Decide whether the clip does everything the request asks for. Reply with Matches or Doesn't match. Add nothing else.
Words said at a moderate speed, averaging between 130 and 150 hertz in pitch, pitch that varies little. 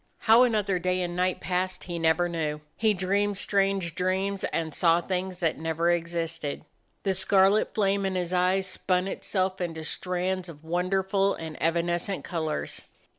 Doesn't match